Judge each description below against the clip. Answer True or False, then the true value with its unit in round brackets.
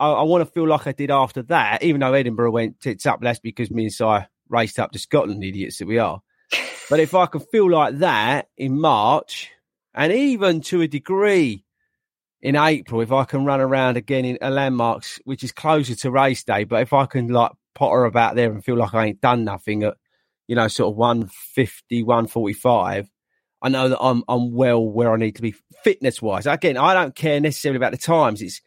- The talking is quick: True (220 wpm)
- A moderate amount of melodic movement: True (3.9 semitones)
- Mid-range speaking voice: False (130 Hz)